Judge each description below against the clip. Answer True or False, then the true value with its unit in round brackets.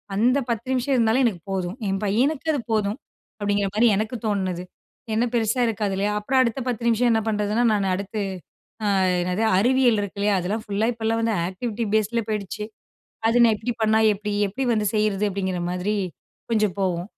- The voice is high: True (215 Hz)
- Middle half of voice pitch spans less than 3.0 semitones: True (2.6 semitones)